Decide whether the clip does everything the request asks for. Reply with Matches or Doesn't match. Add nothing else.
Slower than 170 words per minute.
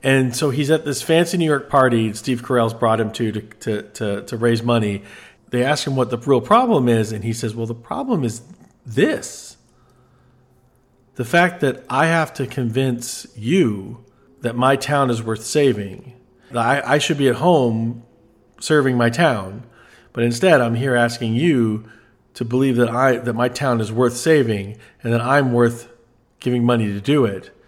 Doesn't match